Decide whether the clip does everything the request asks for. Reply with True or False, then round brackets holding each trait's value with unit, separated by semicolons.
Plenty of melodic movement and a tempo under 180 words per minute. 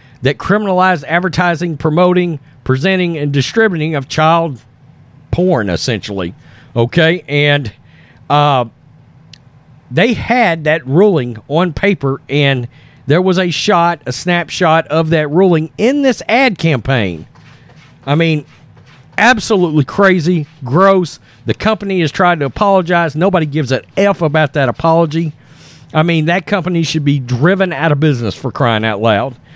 False (4.1 semitones; 135 wpm)